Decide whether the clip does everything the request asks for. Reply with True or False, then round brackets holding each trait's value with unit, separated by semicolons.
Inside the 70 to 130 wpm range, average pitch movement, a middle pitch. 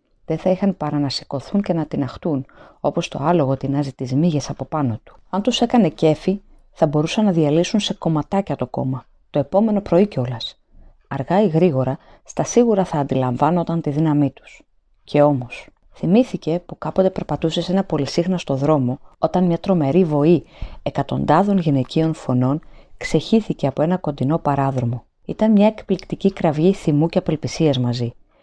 False (155 wpm; 4.9 semitones; 160 Hz)